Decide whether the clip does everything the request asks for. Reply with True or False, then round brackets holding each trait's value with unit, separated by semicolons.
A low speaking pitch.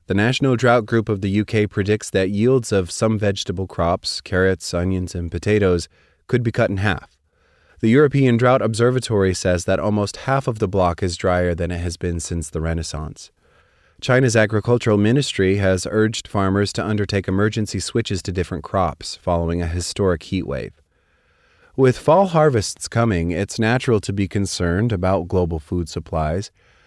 True (100 Hz)